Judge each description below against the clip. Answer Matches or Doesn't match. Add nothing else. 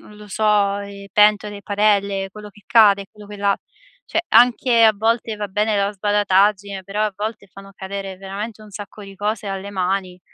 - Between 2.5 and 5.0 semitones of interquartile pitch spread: Doesn't match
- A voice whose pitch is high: Matches